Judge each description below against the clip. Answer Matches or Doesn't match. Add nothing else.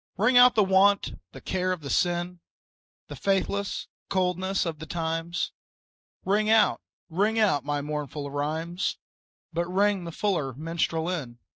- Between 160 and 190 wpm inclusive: Doesn't match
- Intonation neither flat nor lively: Matches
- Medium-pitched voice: Matches